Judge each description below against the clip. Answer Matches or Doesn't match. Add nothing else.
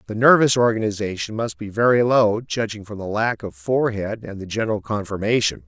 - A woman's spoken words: Doesn't match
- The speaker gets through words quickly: Doesn't match